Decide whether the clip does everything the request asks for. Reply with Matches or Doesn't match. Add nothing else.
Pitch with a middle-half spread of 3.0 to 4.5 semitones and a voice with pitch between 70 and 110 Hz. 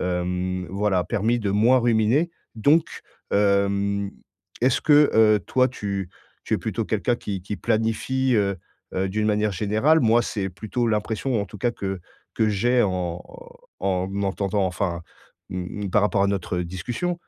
Matches